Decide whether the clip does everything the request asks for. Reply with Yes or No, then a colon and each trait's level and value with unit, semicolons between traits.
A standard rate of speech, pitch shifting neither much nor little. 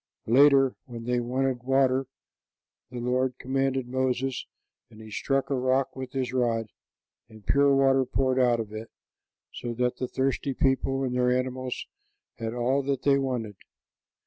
No: average, 155 wpm; narrow, 1.6 semitones